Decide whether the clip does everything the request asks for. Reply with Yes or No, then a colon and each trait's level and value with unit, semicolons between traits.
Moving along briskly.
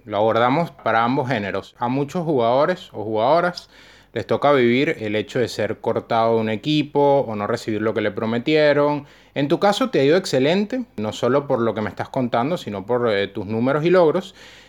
Yes: fast, 205 wpm